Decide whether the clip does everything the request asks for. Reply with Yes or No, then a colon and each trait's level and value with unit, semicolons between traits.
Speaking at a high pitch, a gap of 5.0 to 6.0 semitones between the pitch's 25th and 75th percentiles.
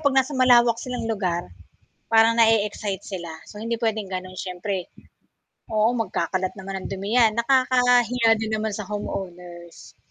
No: high, 215 Hz; average, 3.8 semitones